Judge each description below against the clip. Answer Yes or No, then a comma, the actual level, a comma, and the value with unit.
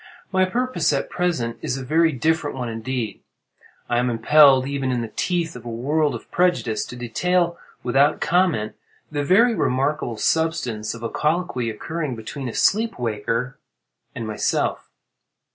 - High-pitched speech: No, low, 135 Hz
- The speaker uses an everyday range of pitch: No, wide, 5.8 semitones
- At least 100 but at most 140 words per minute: No, average, 155 wpm